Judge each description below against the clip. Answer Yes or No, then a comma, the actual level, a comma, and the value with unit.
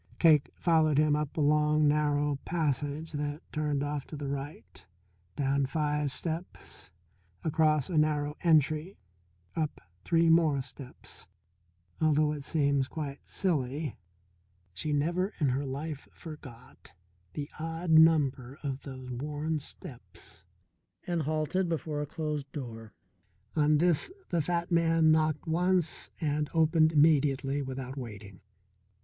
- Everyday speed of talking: No, slow, 125 wpm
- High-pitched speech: No, medium, 150 Hz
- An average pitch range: No, narrow, 2.3 semitones